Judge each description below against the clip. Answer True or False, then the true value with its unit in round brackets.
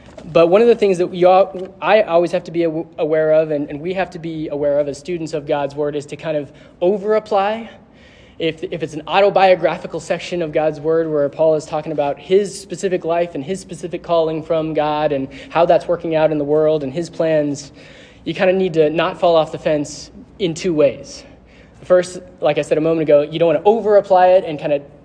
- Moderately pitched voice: True (165 Hz)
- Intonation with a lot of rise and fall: False (3.2 semitones)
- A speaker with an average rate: False (230 wpm)